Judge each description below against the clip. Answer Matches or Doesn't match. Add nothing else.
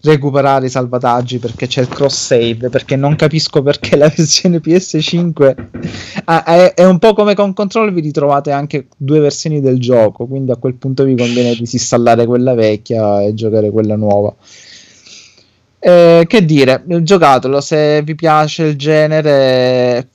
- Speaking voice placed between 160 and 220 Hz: Doesn't match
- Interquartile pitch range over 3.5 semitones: Matches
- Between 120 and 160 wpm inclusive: Matches